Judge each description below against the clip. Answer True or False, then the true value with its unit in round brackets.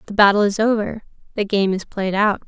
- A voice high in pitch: True (205 Hz)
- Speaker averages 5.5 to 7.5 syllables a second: True (5.6 syllables/s)